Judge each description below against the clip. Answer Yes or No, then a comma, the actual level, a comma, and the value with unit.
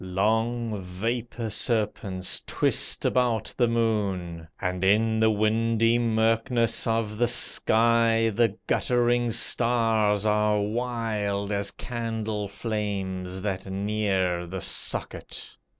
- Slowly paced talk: Yes, slow, 105 wpm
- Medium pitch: No, low, 110 Hz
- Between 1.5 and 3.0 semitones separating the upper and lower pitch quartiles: Yes, narrow, 2.4 semitones